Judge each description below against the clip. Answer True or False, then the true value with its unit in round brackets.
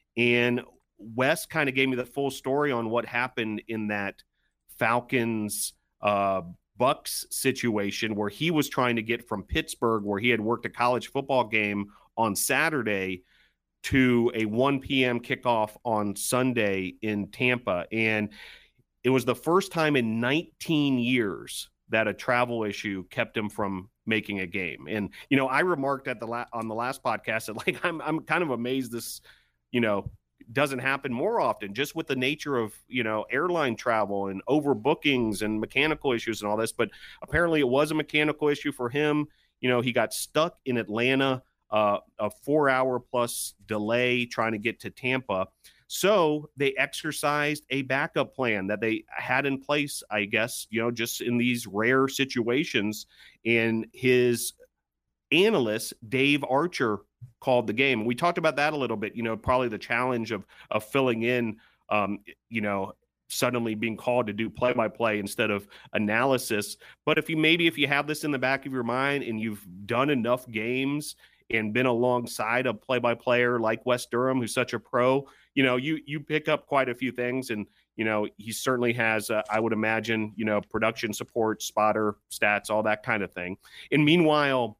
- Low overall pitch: True (120 Hz)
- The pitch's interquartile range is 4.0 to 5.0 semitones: False (3.6 semitones)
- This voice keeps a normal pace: True (185 wpm)